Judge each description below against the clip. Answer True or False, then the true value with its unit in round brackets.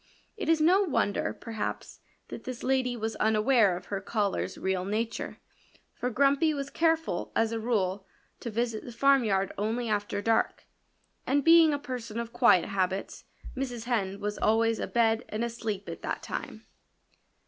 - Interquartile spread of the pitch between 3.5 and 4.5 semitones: True (4.0 semitones)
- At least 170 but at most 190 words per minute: False (160 wpm)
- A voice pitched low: False (230 Hz)